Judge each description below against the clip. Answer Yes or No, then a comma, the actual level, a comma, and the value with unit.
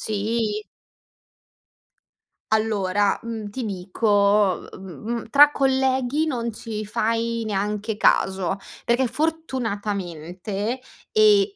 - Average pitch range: Yes, average, 3.5 semitones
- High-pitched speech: Yes, high, 220 Hz